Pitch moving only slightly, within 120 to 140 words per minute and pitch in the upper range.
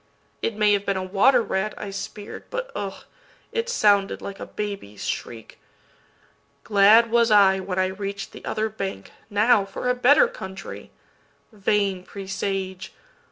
Yes: narrow, 2.1 semitones; slow, 135 wpm; high, 200 Hz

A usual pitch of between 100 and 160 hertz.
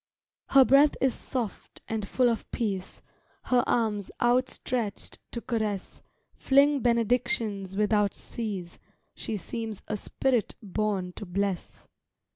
No: high, 220 Hz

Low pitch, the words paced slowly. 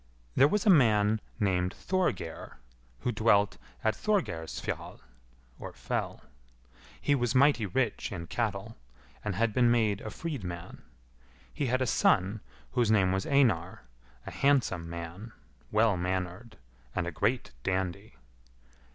Yes: low, 105 Hz; slow, 125 wpm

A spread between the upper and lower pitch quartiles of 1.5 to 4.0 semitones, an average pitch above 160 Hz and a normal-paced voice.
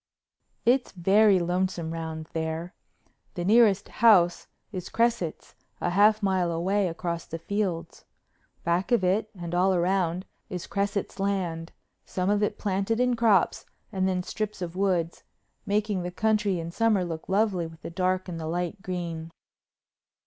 Yes: average, 3.1 semitones; medium, 185 Hz; average, 150 wpm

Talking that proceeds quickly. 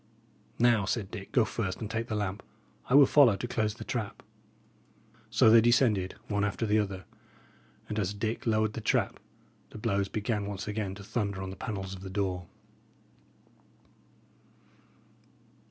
No: average, 160 wpm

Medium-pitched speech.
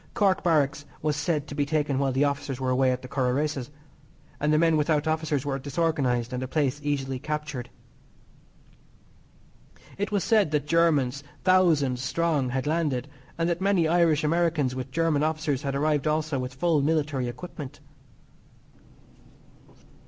Yes: medium, 150 Hz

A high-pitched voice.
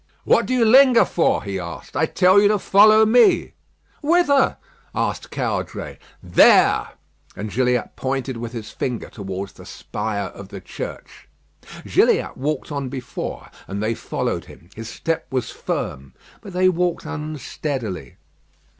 No: low, 135 Hz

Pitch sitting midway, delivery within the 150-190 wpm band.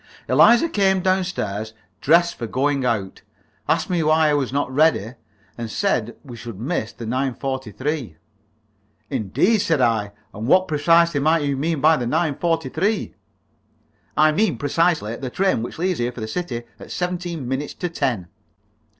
Yes: medium, 145 Hz; average, 160 wpm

